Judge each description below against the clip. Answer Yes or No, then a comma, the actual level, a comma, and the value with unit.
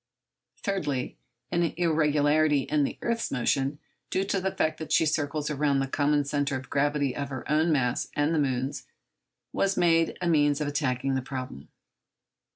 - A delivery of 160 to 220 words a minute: Yes, average, 165 wpm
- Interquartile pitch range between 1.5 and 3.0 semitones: Yes, narrow, 2.5 semitones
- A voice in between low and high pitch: Yes, medium, 145 Hz